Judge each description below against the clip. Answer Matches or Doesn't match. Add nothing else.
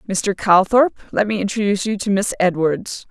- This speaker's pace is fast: Doesn't match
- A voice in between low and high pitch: Doesn't match